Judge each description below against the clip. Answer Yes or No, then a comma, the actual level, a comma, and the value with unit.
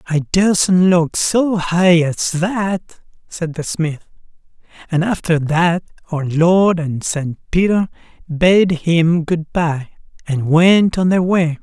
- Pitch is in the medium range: Yes, medium, 170 Hz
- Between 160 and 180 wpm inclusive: No, average, 140 wpm